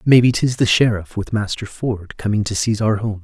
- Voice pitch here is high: No, low, 110 Hz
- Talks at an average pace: No, fast, 220 wpm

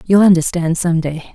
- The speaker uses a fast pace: No, average, 180 wpm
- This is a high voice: No, medium, 170 Hz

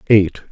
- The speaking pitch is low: Yes, very low, 95 Hz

